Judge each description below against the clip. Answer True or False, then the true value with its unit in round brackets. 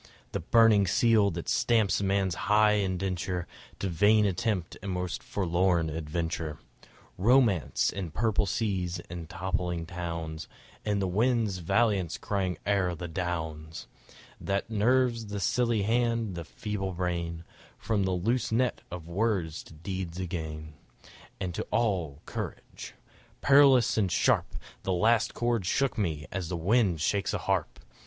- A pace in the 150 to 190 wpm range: False (135 wpm)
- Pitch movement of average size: True (4.0 semitones)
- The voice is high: False (95 Hz)